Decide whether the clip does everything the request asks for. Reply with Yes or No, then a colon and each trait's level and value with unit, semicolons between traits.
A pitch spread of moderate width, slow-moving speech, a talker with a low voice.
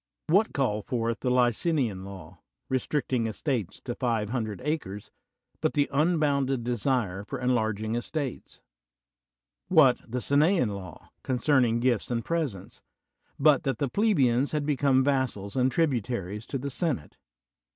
Yes: average, 4.4 semitones; slow, 130 wpm; low, 125 Hz